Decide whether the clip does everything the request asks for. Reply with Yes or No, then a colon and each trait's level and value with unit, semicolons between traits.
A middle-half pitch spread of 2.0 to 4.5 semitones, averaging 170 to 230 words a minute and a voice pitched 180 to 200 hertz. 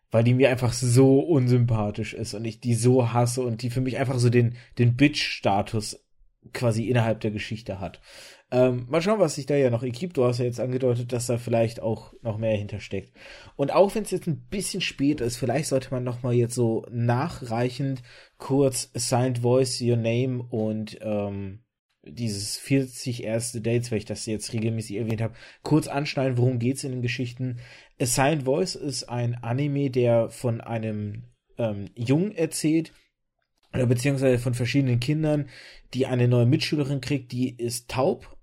No: average, 2.8 semitones; average, 175 wpm; low, 125 Hz